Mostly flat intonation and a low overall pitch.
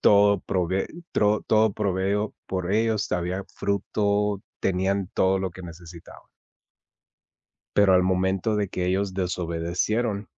Yes: narrow, 2.1 semitones; very low, 95 Hz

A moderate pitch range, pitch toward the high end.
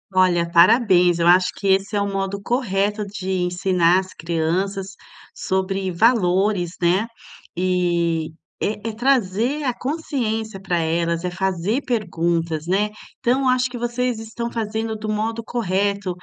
Yes: average, 3.9 semitones; high, 195 Hz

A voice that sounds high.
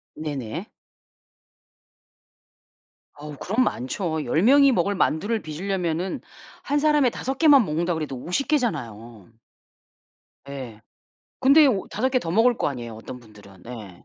No: medium, 165 Hz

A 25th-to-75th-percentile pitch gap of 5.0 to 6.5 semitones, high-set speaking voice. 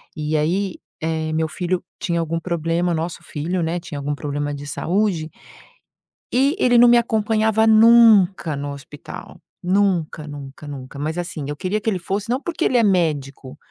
No: wide, 5.4 semitones; medium, 170 Hz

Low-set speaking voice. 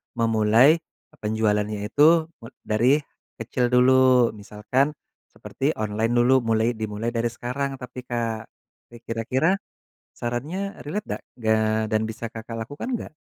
Yes: low, 120 Hz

